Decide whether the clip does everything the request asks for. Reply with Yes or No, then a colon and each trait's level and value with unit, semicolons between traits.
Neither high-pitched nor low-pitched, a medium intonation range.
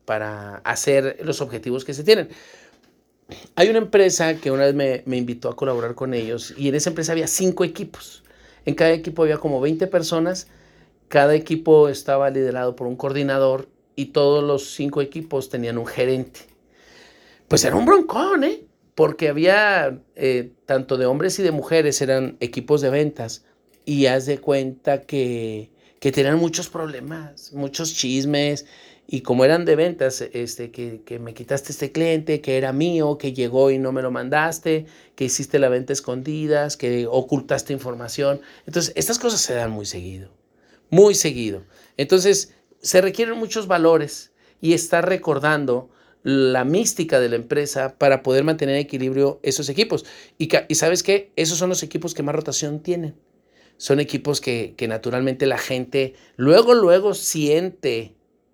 Yes: medium, 145 Hz; average, 3.9 semitones